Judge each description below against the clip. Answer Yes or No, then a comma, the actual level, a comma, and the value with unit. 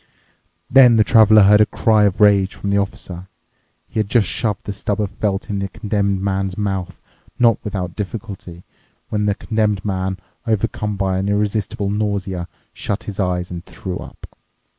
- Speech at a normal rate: Yes, average, 170 wpm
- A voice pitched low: Yes, low, 100 Hz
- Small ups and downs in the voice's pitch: Yes, narrow, 1.7 semitones